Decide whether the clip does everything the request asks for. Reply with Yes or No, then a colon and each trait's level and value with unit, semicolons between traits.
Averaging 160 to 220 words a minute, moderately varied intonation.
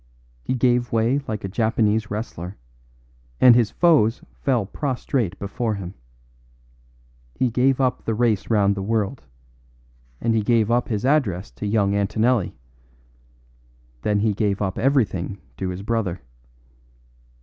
No: slow, 135 wpm; average, 3.4 semitones